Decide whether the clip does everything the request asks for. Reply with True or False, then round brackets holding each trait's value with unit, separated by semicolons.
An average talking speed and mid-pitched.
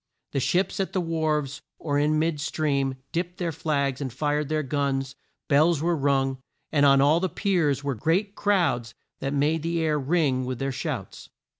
True (180 wpm; 150 Hz)